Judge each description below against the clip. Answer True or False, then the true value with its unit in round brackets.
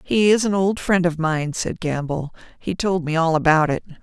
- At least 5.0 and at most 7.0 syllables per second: False (4.8 syllables/s)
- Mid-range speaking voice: True (170 Hz)